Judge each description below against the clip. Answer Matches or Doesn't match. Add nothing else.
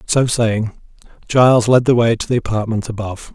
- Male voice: Matches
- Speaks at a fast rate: Doesn't match